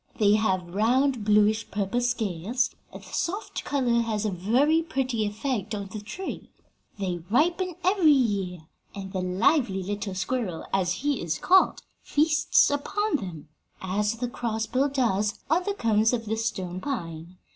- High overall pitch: Yes, high, 220 Hz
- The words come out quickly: No, average, 155 wpm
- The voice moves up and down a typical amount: No, wide, 5.8 semitones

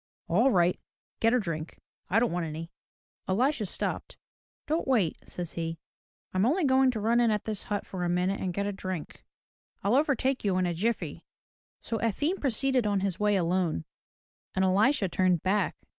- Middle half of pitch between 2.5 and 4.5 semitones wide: No, average, 5.0 semitones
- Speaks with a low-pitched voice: No, high, 200 Hz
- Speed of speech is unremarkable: Yes, average, 180 wpm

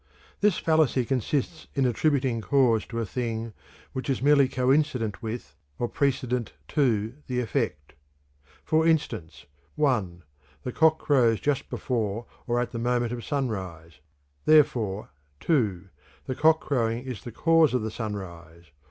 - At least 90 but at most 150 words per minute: Yes, average, 145 wpm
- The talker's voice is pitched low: Yes, low, 125 Hz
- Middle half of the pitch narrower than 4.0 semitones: No, average, 4.3 semitones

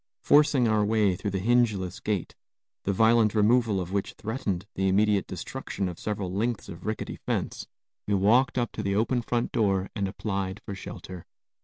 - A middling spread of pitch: Yes, average, 3.0 semitones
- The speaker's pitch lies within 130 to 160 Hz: No, low, 105 Hz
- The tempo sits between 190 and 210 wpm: No, average, 175 wpm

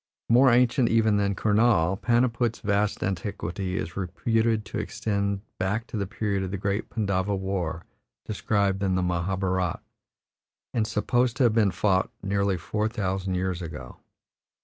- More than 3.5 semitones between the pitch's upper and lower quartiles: No, average, 2.9 semitones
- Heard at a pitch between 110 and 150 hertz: No, low, 100 Hz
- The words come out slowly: No, average, 150 wpm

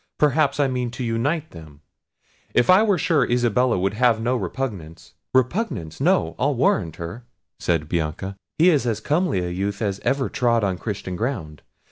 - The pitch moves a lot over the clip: Yes, wide, 6.7 semitones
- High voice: No, low, 120 Hz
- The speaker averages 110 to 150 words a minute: No, average, 165 wpm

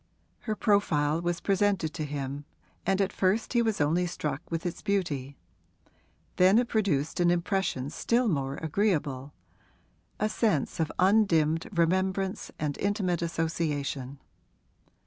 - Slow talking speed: Yes, slow, 125 wpm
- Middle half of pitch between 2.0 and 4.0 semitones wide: No, average, 5.1 semitones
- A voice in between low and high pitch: Yes, medium, 175 Hz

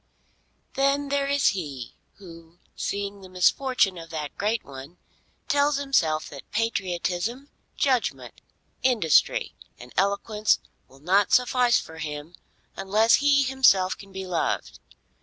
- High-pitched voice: Yes, high, 200 Hz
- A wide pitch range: Yes, wide, 7.4 semitones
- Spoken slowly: Yes, slow, 120 wpm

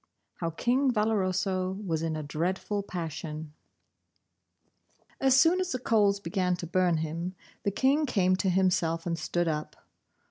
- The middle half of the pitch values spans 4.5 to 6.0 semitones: No, average, 4.1 semitones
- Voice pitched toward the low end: No, medium, 185 Hz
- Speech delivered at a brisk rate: No, average, 150 wpm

